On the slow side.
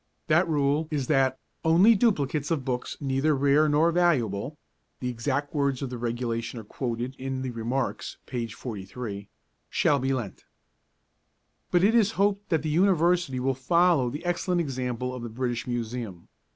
No: average, 165 wpm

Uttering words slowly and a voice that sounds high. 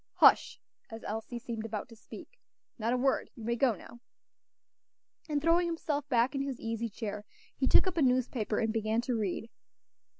No: average, 180 wpm; high, 235 Hz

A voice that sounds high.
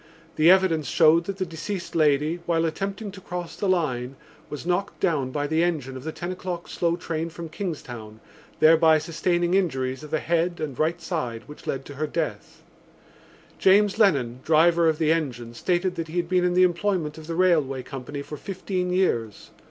No: medium, 165 Hz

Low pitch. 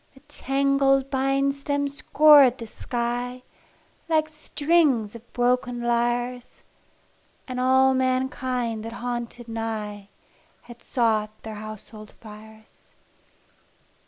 No: high, 245 Hz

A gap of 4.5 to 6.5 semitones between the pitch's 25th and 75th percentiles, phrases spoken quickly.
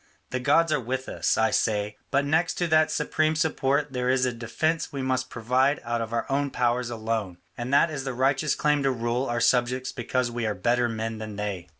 No: average, 3.3 semitones; fast, 220 wpm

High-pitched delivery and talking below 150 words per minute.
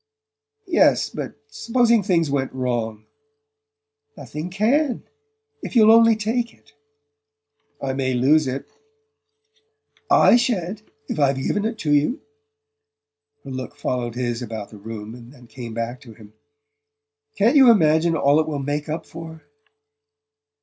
No: medium, 150 Hz; average, 140 wpm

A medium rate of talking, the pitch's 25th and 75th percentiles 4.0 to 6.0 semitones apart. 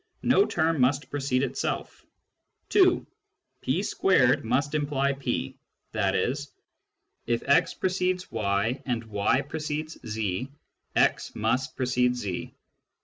No: slow, 110 wpm; average, 4.3 semitones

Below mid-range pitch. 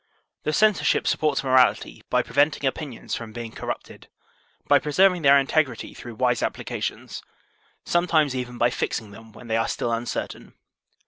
Yes: low, 130 Hz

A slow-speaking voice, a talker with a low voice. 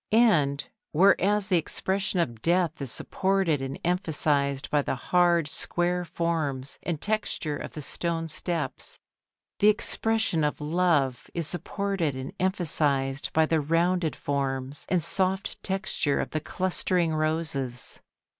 No: slow, 130 wpm; medium, 165 Hz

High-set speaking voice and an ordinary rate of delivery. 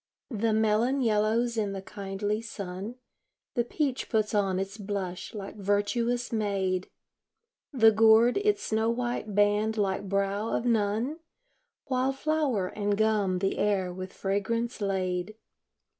No: high, 210 Hz; slow, 130 wpm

